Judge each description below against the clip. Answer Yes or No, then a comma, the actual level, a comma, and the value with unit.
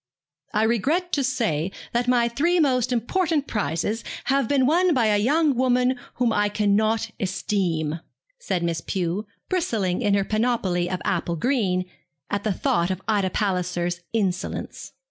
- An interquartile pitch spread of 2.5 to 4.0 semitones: No, wide, 5.5 semitones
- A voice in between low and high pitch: No, high, 215 Hz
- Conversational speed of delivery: Yes, average, 150 wpm